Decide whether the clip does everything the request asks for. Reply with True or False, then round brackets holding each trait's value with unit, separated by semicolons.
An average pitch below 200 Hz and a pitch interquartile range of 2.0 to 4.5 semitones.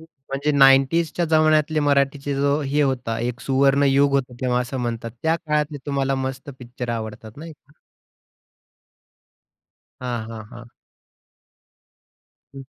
True (135 Hz; 2.8 semitones)